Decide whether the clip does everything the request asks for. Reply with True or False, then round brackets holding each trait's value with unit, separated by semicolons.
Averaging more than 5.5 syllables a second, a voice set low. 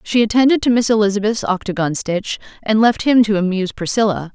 False (6.0 syllables/s; 210 Hz)